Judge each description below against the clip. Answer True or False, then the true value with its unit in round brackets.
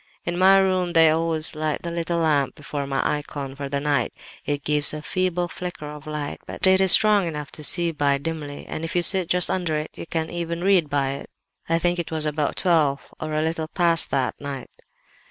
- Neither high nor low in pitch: True (160 Hz)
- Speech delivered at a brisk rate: True (220 wpm)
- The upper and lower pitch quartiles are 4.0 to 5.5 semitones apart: False (2.9 semitones)